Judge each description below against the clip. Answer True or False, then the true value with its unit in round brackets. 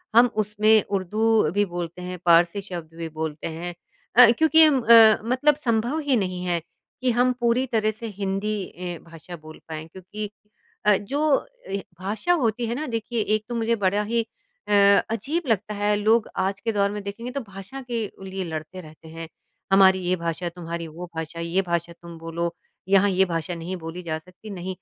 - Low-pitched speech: False (195 Hz)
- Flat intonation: False (4.7 semitones)